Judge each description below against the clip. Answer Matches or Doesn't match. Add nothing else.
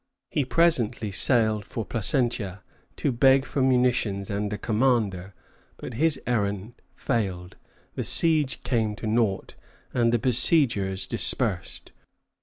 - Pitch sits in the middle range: Doesn't match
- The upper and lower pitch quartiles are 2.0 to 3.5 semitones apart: Doesn't match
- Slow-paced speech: Matches